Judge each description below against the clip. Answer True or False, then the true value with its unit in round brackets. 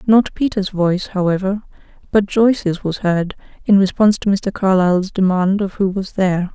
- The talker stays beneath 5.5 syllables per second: True (5.2 syllables/s)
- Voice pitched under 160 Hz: False (195 Hz)